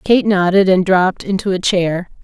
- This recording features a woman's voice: Yes, female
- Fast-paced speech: No, average, 190 wpm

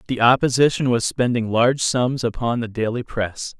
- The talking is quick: No, average, 165 wpm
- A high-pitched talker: No, low, 120 Hz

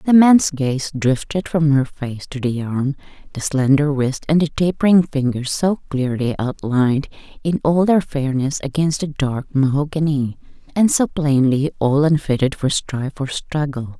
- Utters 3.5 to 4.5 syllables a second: Yes, 4.4 syllables/s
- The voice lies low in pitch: No, medium, 145 Hz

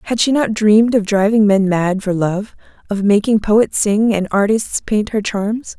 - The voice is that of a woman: Yes, female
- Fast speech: No, average, 195 wpm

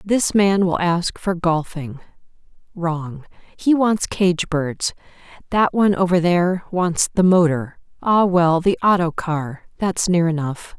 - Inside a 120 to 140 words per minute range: Yes, slow, 135 wpm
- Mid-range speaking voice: Yes, medium, 175 Hz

